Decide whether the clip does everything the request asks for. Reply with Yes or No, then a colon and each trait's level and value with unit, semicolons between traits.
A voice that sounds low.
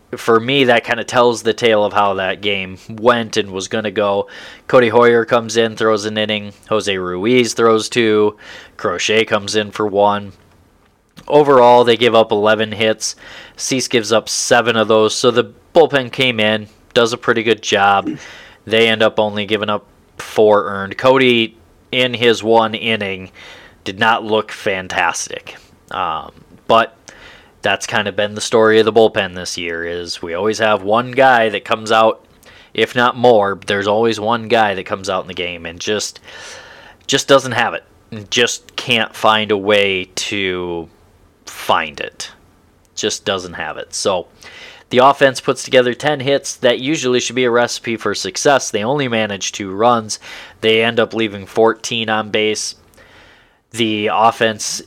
Yes: low, 110 Hz